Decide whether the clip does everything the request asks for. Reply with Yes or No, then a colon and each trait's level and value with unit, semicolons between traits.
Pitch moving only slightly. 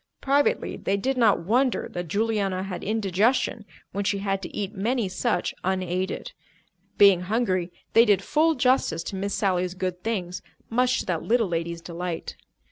No: average, 4.0 semitones